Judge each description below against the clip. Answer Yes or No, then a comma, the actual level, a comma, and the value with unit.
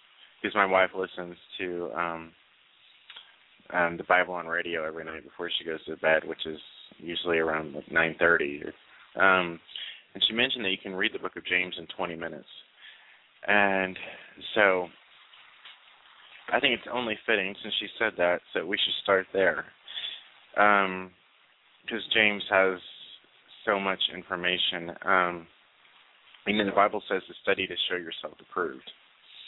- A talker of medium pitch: No, very low, 90 Hz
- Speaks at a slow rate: No, average, 155 wpm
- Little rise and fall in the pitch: Yes, narrow, 2.3 semitones